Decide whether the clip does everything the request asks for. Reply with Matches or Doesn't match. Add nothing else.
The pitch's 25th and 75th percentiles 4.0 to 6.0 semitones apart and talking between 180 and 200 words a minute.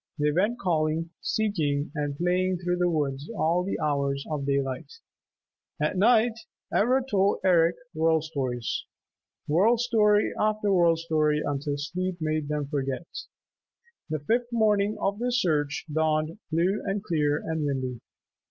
Doesn't match